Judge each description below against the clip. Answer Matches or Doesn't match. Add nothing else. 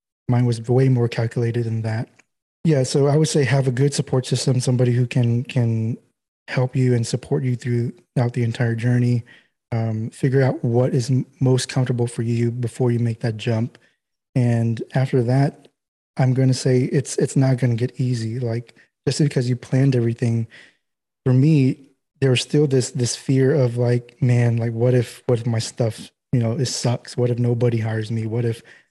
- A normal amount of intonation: Doesn't match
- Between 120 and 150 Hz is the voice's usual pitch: Matches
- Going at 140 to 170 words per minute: Doesn't match